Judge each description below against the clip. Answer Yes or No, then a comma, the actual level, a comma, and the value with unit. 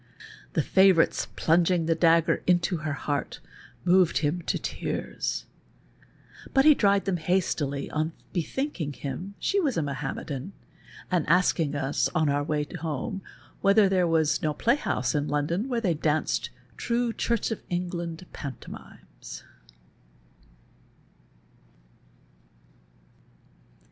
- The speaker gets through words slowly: Yes, slow, 120 wpm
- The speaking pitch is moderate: Yes, medium, 170 Hz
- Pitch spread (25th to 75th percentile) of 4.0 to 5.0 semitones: Yes, average, 4.3 semitones